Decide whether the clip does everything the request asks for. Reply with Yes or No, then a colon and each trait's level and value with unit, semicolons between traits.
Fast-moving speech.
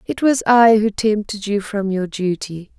No: average, 195 wpm